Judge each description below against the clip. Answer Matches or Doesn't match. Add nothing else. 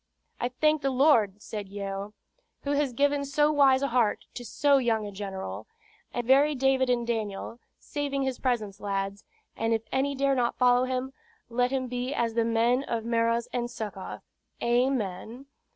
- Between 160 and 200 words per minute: Matches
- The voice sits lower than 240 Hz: Doesn't match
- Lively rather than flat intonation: Doesn't match